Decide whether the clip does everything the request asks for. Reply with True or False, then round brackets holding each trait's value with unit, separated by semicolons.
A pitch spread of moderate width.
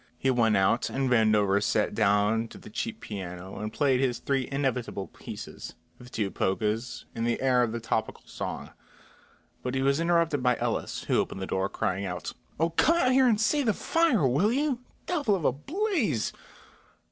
False (8.3 semitones)